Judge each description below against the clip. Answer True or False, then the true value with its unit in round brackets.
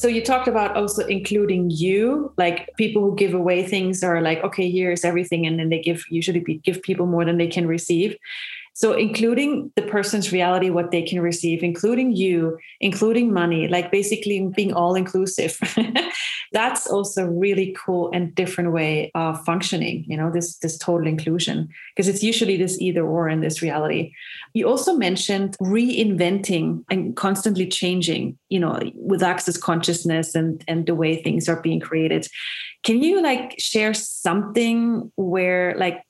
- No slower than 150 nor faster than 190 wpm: True (165 wpm)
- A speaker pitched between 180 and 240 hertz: True (185 Hz)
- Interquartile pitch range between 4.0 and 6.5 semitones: False (3.5 semitones)